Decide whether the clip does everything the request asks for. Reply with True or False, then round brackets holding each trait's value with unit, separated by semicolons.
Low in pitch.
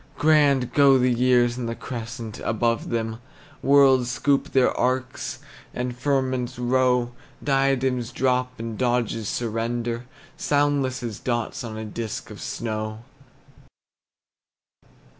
True (125 Hz)